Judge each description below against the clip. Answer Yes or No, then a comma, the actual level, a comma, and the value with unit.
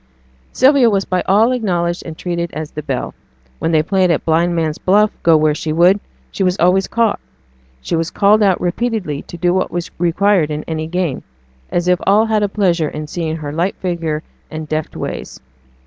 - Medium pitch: Yes, medium, 175 Hz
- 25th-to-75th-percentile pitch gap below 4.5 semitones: Yes, average, 3.7 semitones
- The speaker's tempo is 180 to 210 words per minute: Yes, average, 195 wpm